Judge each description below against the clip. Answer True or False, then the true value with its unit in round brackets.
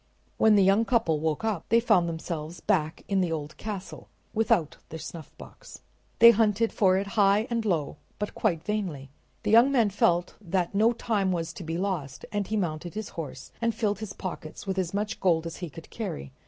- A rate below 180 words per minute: False (200 wpm)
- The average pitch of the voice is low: False (190 Hz)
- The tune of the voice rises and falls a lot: False (4.5 semitones)